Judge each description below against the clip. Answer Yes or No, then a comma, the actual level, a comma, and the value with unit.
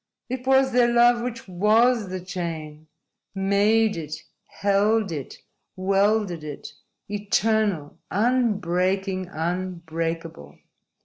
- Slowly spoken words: Yes, slow, 90 wpm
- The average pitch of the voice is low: No, high, 195 Hz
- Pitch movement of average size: Yes, average, 4.6 semitones